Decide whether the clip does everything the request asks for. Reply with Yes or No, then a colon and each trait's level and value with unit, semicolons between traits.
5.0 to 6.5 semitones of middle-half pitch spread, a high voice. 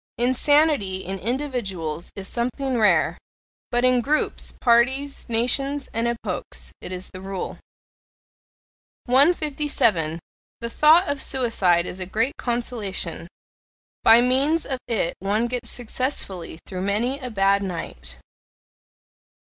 Yes: wide, 5.5 semitones; high, 235 Hz